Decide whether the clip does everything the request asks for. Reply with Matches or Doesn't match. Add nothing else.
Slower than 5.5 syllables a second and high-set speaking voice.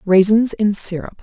Matches